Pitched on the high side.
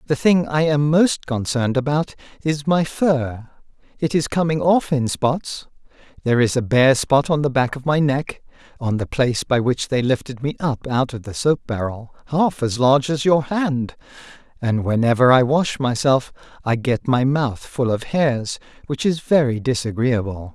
No: low, 135 Hz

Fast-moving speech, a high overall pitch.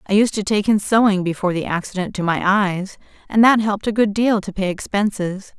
Yes: fast, 225 wpm; high, 200 Hz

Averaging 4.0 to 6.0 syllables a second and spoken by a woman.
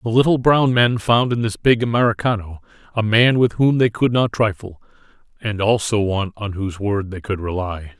No: 5.1 syllables/s; male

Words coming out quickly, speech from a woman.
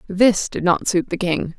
Yes: fast, 225 wpm; female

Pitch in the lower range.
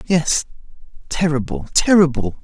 No: medium, 150 Hz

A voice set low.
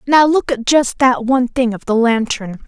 No: very high, 250 Hz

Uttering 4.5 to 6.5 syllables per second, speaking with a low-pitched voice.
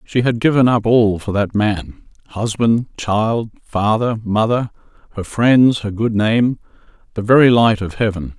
No: 4.1 syllables/s; low, 110 Hz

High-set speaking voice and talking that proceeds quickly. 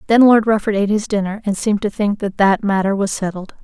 Yes: high, 205 Hz; fast, 250 wpm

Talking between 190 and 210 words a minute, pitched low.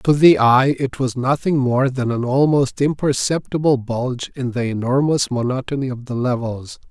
No: average, 165 wpm; low, 130 Hz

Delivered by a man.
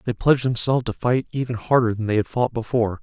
Yes: male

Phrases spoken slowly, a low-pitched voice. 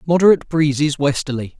No: slow, 115 wpm; medium, 145 Hz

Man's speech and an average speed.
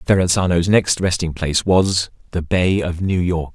Yes: male; average, 170 wpm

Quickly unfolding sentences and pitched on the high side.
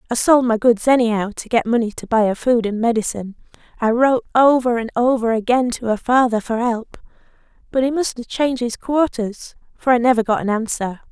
Yes: fast, 210 wpm; high, 235 Hz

